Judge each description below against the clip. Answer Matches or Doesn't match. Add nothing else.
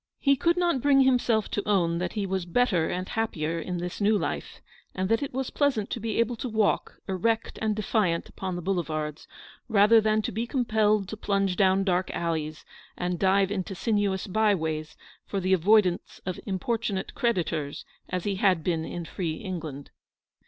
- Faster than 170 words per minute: Matches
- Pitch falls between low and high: Doesn't match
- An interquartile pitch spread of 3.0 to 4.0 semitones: Matches